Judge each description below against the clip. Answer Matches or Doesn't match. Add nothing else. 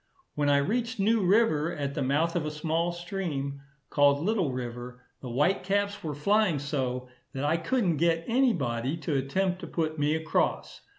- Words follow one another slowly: Doesn't match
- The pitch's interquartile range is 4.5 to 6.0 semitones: Matches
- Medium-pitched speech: Matches